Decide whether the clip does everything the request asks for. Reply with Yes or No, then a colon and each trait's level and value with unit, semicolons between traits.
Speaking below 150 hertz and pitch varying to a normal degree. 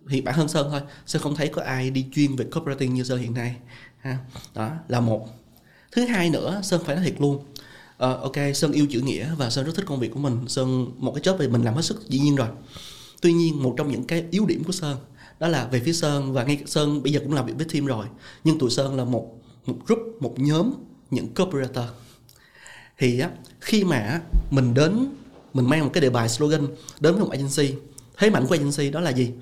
Yes: medium, 140 Hz; average, 4.0 semitones